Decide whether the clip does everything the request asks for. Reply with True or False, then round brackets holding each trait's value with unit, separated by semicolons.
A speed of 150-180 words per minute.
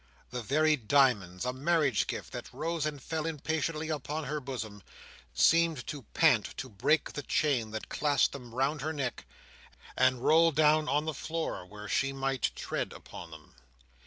True (160 wpm)